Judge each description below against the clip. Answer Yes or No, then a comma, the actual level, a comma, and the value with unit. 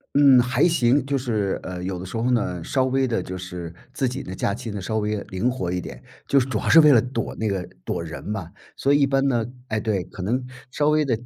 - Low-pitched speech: Yes, low, 115 Hz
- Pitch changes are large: Yes, wide, 6.0 semitones